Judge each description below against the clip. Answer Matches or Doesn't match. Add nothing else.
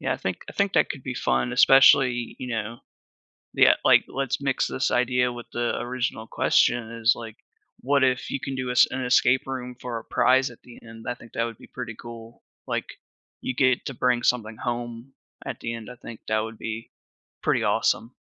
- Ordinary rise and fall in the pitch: Doesn't match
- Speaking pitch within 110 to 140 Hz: Matches